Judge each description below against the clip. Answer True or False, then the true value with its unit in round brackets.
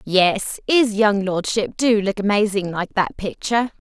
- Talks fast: False (155 wpm)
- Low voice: False (205 Hz)